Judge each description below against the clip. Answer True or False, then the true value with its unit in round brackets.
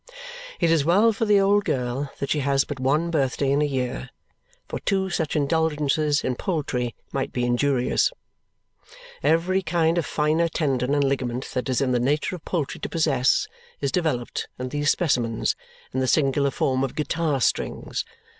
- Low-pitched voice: False (145 Hz)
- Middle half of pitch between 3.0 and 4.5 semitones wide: True (4.0 semitones)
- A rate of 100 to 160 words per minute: False (175 wpm)